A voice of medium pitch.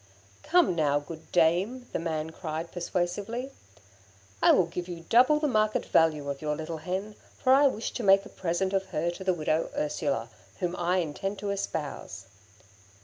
Yes: medium, 180 Hz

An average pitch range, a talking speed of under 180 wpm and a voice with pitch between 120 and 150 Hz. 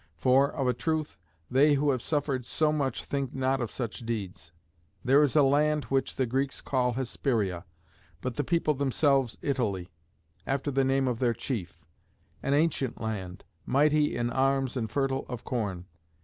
Yes: average, 3.1 semitones; average, 165 wpm; low, 135 Hz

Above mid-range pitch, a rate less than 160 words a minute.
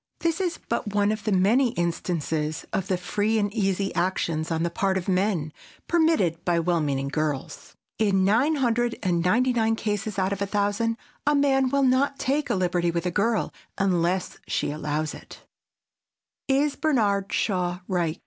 No: high, 195 Hz; average, 175 wpm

